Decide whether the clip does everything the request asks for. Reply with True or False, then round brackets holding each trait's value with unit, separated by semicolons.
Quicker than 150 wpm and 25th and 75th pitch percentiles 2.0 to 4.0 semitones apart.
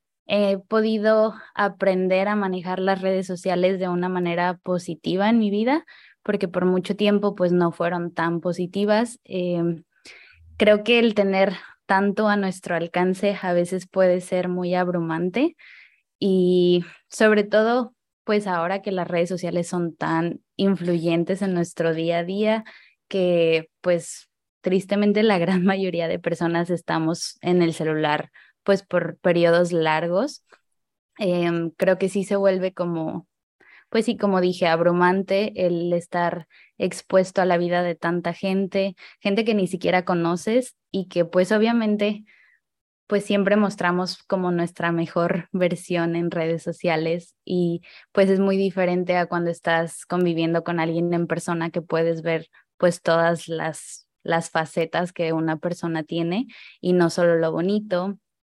False (145 wpm; 2.4 semitones)